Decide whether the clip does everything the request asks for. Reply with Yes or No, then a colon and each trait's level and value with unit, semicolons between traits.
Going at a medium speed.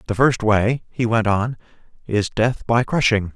Yes: average, 180 wpm